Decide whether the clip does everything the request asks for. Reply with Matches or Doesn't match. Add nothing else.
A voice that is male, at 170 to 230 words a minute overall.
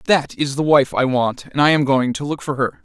Doesn't match